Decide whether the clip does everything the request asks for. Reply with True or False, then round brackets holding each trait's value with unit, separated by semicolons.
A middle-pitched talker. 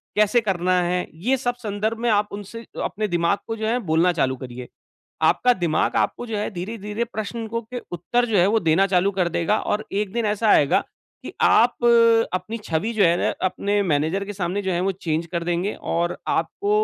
False (200 Hz)